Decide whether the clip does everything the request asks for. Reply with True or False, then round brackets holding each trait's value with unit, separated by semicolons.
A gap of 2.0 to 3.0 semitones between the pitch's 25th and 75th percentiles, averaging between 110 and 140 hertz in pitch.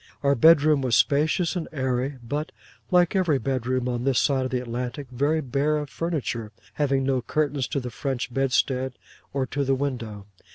True (2.7 semitones; 135 Hz)